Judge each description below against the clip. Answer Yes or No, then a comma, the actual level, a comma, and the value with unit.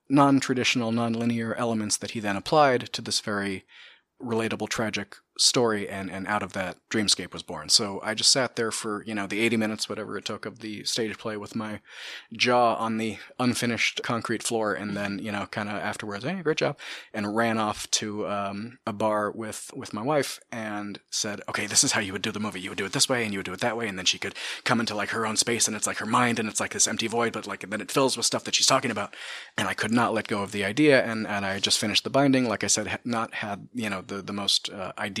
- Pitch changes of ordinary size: No, narrow, 2.2 semitones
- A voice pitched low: Yes, low, 110 Hz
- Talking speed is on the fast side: Yes, fast, 265 wpm